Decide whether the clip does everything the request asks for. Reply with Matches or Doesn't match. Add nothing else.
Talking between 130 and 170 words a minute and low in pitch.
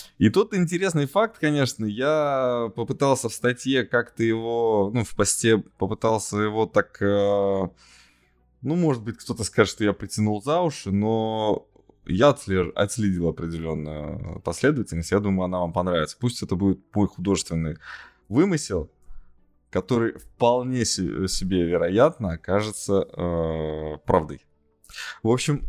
Doesn't match